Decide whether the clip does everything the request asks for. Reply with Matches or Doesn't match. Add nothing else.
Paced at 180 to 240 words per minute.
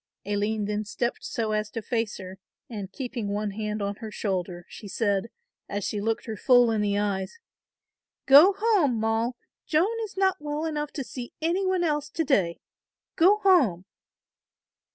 Doesn't match